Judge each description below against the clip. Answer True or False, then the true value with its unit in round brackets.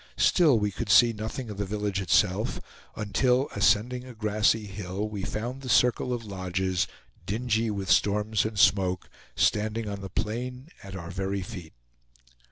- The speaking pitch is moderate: False (105 Hz)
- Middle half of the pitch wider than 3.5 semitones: False (3.0 semitones)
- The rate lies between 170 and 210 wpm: False (160 wpm)